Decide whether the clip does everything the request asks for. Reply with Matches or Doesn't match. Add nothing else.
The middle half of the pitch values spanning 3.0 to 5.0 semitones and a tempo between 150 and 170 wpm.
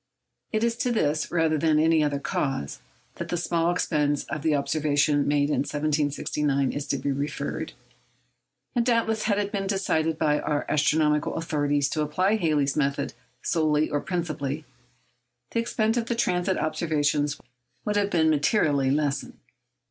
Matches